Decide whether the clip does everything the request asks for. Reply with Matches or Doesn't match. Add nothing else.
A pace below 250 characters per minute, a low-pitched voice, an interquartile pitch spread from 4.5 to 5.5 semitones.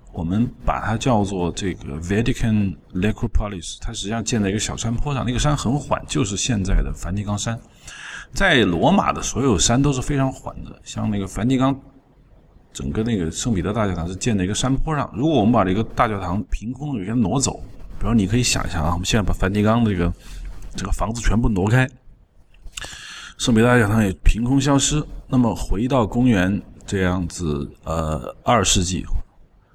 Doesn't match